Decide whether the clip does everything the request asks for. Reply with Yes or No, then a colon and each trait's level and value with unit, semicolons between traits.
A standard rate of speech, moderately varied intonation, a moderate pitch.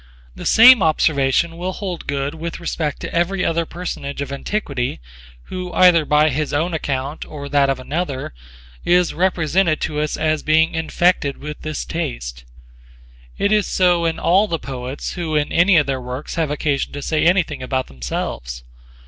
Yes: average, 170 wpm; average, 3.7 semitones; medium, 155 Hz